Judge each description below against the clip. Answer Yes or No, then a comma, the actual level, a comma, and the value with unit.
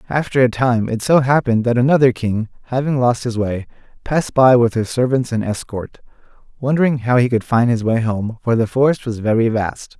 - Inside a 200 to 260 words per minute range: Yes, fast, 205 wpm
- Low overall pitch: Yes, low, 120 Hz